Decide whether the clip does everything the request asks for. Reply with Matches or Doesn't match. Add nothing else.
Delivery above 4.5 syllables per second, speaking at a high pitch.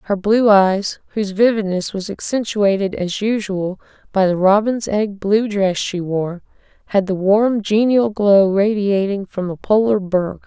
Doesn't match